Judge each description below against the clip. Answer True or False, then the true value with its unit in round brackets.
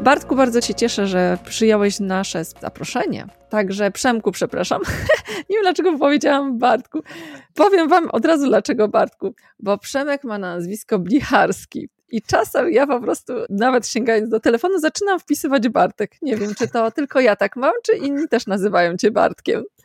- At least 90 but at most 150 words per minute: False (160 wpm)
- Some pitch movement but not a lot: False (5.7 semitones)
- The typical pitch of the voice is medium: False (235 Hz)